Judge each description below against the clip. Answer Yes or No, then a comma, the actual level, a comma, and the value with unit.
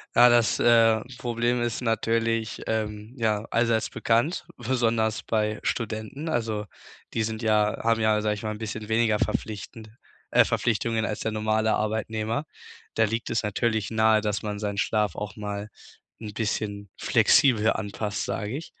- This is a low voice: Yes, low, 110 Hz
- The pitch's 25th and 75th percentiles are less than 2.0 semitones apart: Yes, narrow, 1.3 semitones